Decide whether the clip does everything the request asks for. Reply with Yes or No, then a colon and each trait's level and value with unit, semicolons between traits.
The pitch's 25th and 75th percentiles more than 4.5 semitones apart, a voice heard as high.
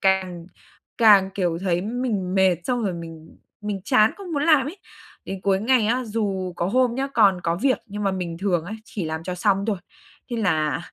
No: average, 4.2 semitones; high, 195 Hz